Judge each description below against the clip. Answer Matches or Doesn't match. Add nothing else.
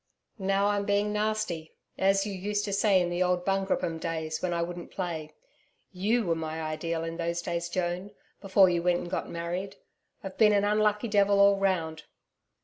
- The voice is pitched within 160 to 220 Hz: Matches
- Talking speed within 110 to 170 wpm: Doesn't match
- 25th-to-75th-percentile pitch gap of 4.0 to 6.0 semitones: Doesn't match